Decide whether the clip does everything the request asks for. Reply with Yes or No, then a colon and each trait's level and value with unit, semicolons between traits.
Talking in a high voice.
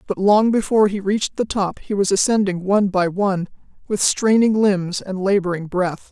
Yes: high, 195 Hz